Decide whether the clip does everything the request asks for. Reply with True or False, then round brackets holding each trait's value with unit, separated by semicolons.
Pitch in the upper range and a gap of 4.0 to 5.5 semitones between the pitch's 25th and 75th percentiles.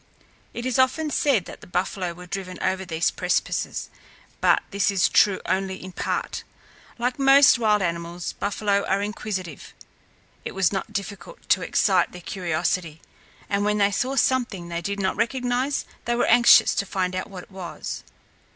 True (195 Hz; 4.5 semitones)